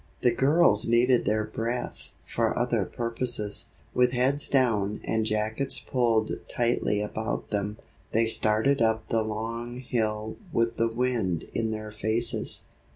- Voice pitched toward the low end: Yes, low, 115 Hz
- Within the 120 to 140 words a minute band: Yes, slow, 135 wpm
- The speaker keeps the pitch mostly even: Yes, narrow, 2.1 semitones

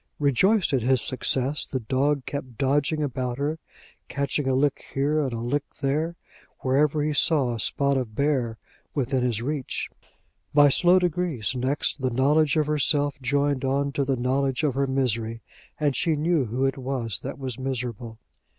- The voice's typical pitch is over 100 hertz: Yes, low, 135 Hz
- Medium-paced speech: Yes, average, 170 wpm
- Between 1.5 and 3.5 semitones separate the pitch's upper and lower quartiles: Yes, narrow, 2.5 semitones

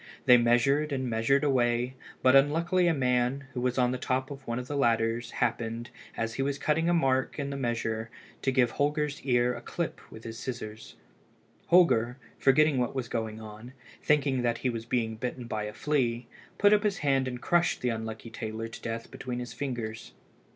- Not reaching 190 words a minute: No, average, 195 wpm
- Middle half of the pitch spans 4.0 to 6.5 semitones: No, average, 3.1 semitones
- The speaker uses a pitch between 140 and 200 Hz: No, low, 125 Hz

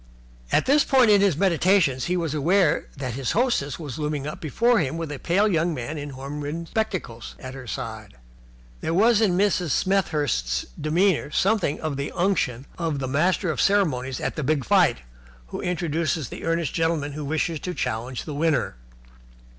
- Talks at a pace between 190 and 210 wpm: No, average, 180 wpm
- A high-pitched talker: No, medium, 160 Hz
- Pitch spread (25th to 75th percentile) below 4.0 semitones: No, average, 4.7 semitones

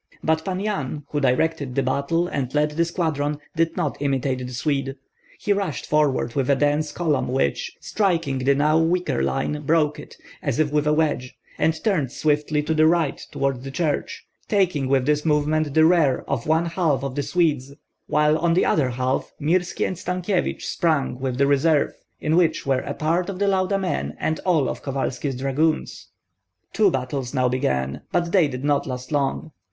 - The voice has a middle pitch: Yes, medium, 150 Hz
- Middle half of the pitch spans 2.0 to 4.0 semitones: Yes, average, 3.5 semitones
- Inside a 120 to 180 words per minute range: No, average, 190 wpm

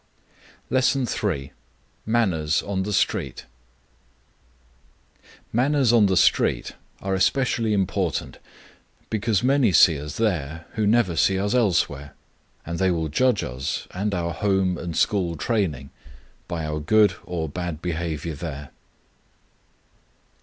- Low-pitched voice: Yes, very low, 95 Hz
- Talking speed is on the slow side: Yes, slow, 125 wpm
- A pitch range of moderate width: Yes, average, 5.0 semitones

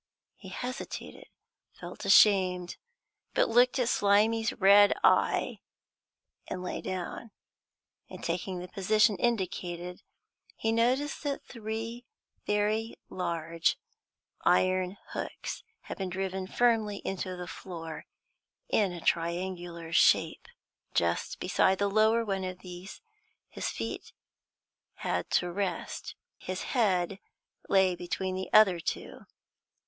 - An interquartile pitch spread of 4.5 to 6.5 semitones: No, average, 3.3 semitones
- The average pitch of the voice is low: No, high, 190 Hz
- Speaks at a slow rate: Yes, slow, 110 wpm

